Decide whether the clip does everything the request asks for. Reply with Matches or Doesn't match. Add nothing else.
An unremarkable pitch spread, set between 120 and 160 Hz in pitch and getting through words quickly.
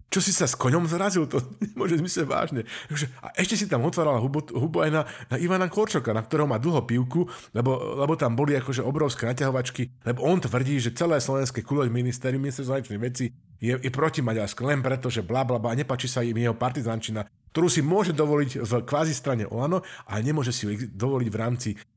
Matches